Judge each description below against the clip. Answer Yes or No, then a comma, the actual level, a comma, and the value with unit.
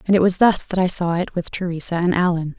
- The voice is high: No, medium, 175 Hz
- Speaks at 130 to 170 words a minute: No, fast, 280 wpm